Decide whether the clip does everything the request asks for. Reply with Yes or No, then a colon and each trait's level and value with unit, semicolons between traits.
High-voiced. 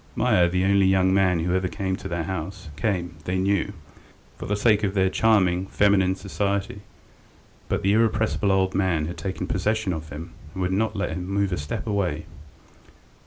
No: very low, 95 Hz